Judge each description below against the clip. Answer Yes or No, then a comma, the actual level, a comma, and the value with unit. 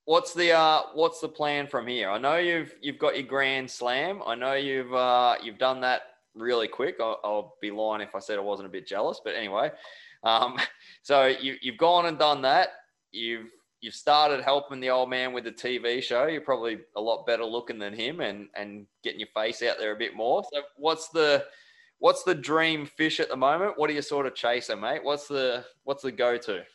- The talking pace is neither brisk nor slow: No, fast, 220 wpm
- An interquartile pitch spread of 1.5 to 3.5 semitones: No, average, 3.9 semitones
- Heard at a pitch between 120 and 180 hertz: Yes, low, 135 Hz